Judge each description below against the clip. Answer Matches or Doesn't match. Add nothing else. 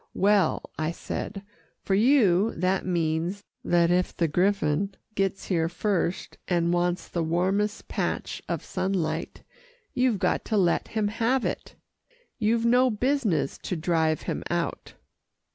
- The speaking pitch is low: Doesn't match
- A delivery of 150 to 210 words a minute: Doesn't match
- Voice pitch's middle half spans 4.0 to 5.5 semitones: Doesn't match